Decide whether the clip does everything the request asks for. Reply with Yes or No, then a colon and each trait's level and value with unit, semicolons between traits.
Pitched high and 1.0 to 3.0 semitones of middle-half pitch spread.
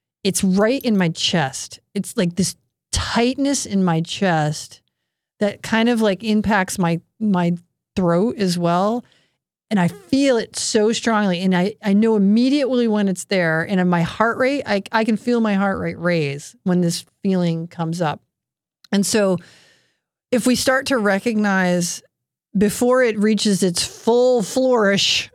No: high, 200 Hz; average, 4.3 semitones